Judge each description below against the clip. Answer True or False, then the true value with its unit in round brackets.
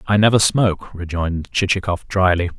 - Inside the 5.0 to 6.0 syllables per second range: True (5.6 syllables/s)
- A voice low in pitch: True (95 Hz)